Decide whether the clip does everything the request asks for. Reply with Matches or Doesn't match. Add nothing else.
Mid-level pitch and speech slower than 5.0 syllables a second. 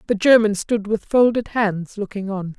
Doesn't match